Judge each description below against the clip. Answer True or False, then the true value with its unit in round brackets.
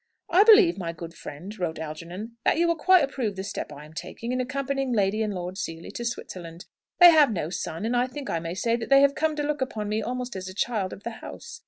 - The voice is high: True (225 Hz)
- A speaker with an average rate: False (255 wpm)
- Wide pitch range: True (7.2 semitones)